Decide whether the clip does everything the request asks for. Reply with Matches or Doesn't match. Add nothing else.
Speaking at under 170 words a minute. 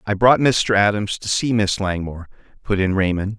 Doesn't match